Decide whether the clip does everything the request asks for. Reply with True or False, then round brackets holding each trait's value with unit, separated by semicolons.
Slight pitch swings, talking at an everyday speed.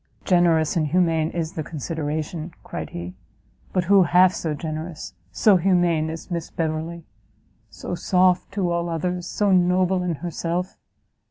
True (2.2 semitones; 145 wpm)